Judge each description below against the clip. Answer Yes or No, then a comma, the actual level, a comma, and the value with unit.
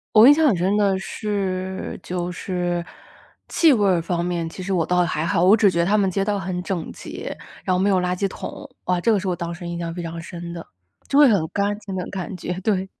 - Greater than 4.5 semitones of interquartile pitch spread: No, narrow, 2.5 semitones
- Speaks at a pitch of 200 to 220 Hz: No, medium, 185 Hz